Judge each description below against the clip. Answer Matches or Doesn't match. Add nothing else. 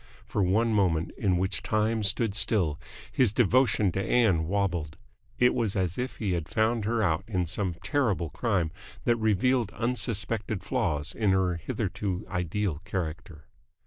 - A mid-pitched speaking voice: Doesn't match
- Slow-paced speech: Doesn't match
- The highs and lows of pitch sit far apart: Doesn't match